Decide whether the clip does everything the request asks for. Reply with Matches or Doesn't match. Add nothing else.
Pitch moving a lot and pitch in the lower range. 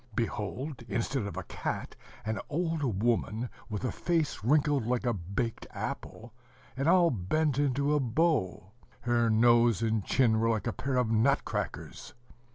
Doesn't match